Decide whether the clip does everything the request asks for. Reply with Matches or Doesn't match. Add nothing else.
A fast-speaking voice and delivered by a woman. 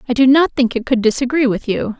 Matches